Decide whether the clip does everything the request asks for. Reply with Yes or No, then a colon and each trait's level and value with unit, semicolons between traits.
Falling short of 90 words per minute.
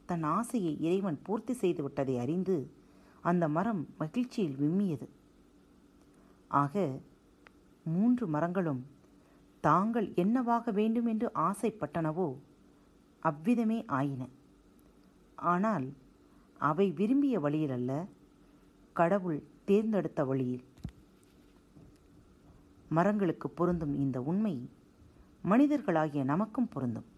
Yes: average, 80 wpm